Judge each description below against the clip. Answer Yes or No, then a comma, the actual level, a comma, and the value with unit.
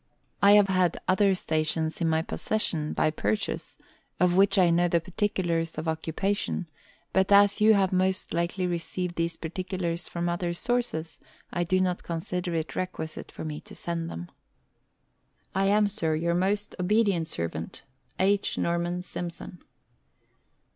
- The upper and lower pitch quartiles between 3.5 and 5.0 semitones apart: No, narrow, 2.6 semitones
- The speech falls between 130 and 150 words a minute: Yes, average, 145 wpm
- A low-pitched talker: No, medium, 175 Hz